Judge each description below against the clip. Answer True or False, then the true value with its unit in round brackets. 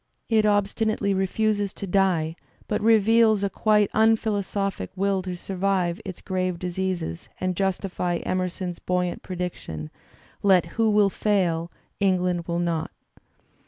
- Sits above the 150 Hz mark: True (190 Hz)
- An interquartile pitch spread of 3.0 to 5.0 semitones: False (2.4 semitones)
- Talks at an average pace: False (125 wpm)